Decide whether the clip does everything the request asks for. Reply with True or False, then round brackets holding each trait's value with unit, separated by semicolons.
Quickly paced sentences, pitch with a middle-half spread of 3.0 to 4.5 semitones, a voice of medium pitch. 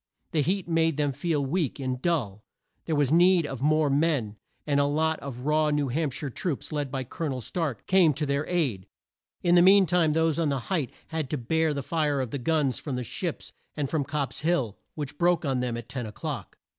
True (225 wpm; 3.4 semitones; 150 Hz)